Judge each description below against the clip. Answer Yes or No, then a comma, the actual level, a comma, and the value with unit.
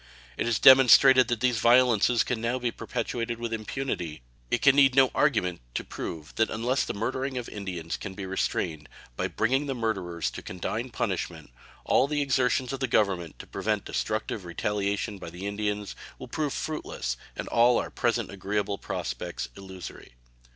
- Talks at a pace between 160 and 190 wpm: Yes, average, 170 wpm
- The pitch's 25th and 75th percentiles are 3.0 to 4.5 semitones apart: No, average, 4.9 semitones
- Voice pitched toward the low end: Yes, low, 115 Hz